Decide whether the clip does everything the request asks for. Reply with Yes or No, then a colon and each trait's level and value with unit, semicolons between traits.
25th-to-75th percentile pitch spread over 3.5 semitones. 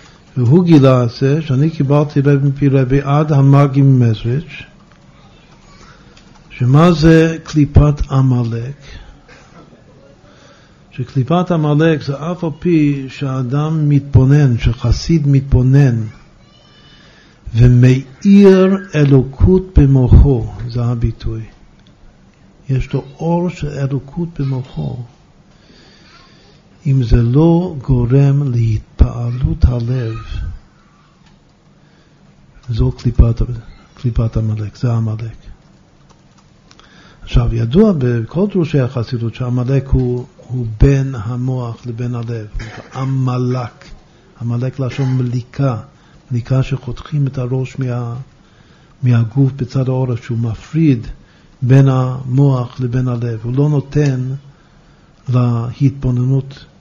No: average, 2.8 semitones